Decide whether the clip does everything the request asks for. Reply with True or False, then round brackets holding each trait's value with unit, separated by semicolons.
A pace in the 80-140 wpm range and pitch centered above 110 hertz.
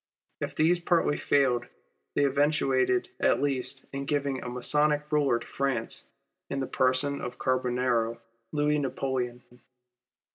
True (135 wpm; 140 Hz)